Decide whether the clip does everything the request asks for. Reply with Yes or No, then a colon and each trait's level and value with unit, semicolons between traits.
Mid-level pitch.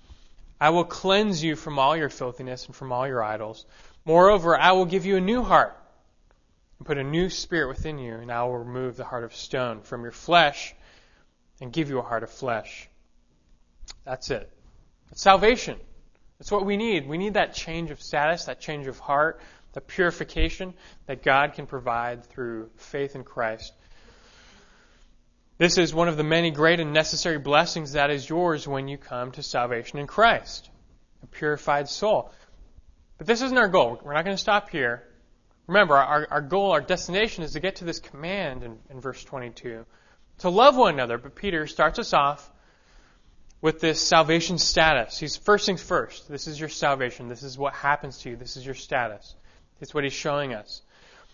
Yes: medium, 145 Hz